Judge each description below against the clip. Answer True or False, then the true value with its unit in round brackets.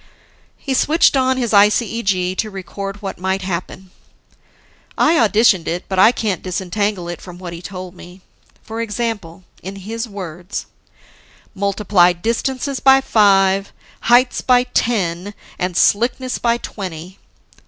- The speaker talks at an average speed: False (130 wpm)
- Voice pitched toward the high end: True (200 Hz)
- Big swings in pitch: False (4.1 semitones)